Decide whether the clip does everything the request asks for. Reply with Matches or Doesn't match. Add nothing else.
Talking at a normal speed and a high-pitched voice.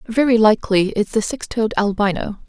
Matches